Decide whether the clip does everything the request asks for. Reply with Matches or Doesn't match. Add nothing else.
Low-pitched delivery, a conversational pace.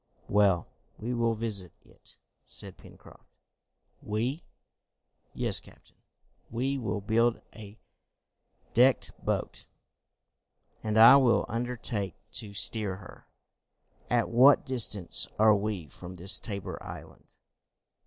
Doesn't match